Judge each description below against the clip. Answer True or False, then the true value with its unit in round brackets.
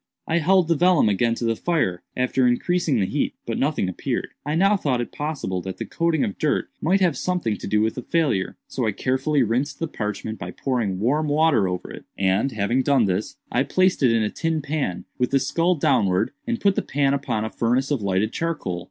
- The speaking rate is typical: False (220 wpm)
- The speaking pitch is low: True (130 Hz)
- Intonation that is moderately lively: False (6.8 semitones)